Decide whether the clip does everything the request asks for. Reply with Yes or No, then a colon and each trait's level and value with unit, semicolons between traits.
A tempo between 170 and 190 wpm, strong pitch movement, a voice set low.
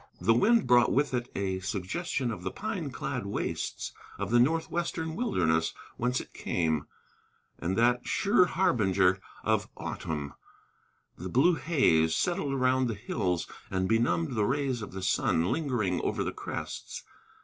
No: average, 150 wpm; wide, 7.2 semitones; low, 120 Hz